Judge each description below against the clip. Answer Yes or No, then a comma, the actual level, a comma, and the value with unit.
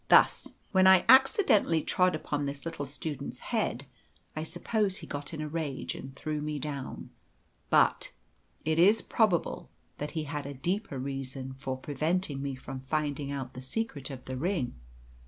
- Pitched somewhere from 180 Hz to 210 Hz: No, medium, 150 Hz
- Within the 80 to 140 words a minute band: No, average, 165 wpm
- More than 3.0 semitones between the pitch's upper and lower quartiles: Yes, average, 4.2 semitones